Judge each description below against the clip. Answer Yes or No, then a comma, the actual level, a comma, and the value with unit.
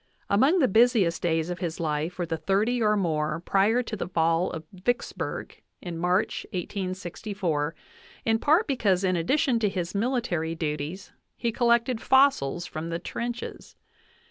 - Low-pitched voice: No, medium, 185 Hz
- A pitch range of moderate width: No, wide, 5.7 semitones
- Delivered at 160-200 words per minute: No, average, 150 wpm